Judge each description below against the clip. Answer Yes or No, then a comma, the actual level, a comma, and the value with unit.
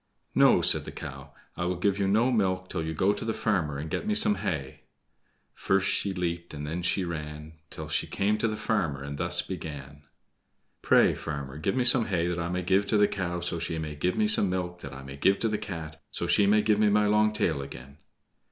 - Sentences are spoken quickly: Yes, fast, 235 wpm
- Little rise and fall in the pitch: No, average, 5.0 semitones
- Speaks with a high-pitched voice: No, very low, 90 Hz